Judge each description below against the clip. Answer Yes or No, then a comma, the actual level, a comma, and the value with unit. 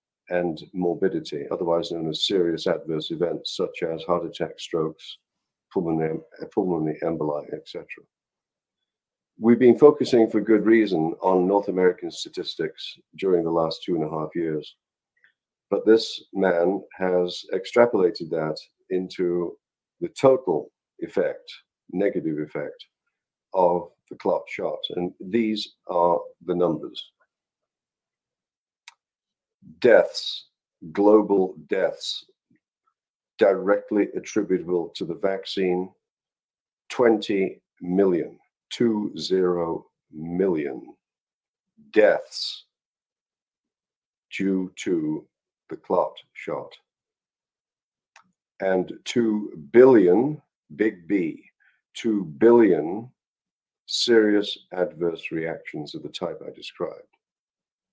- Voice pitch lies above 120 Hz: No, low, 105 Hz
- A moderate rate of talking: No, slow, 95 wpm